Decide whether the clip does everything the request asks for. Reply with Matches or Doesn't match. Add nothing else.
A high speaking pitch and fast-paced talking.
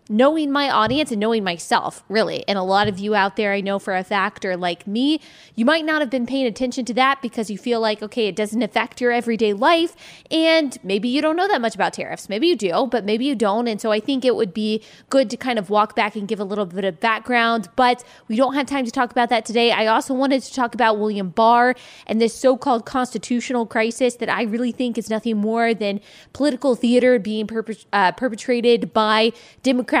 Matches